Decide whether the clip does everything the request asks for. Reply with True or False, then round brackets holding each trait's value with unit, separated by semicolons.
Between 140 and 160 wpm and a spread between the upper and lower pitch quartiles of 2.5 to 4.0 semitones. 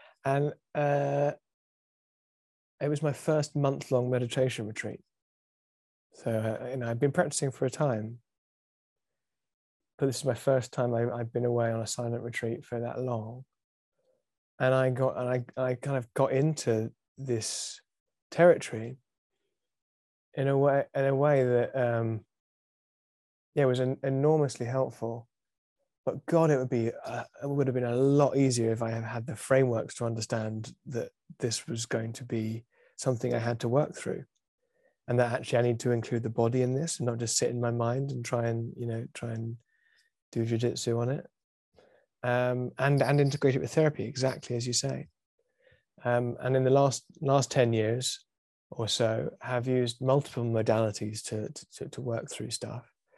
False (175 wpm; 2.9 semitones)